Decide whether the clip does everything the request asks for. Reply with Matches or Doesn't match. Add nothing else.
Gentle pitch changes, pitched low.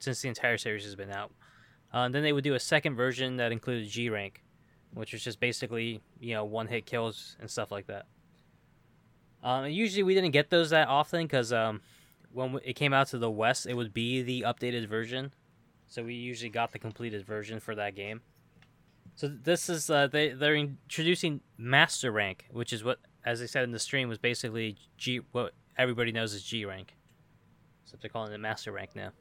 Doesn't match